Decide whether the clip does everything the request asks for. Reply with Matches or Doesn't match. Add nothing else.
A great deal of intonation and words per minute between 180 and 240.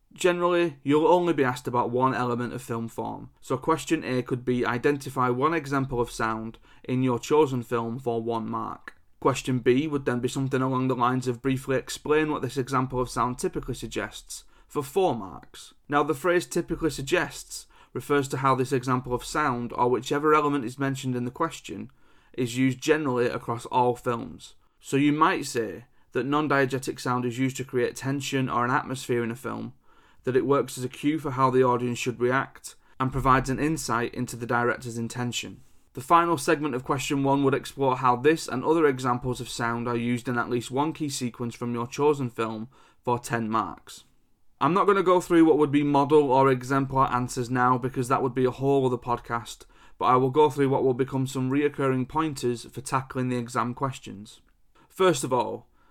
Doesn't match